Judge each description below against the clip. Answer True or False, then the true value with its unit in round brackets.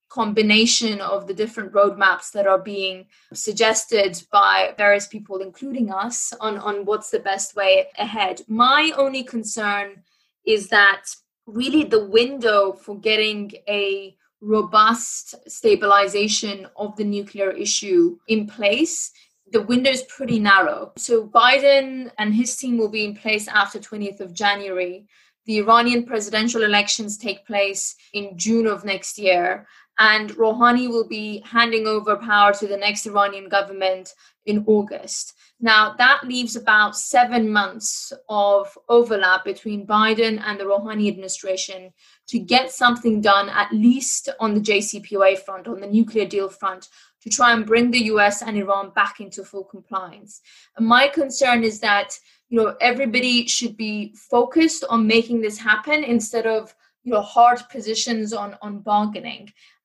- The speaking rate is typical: True (150 wpm)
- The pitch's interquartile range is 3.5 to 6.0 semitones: False (2.6 semitones)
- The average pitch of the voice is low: False (215 Hz)